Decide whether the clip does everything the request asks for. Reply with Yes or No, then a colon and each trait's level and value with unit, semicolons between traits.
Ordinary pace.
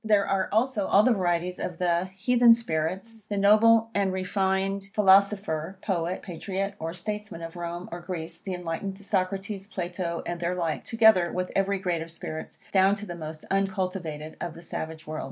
Yes: average, 175 wpm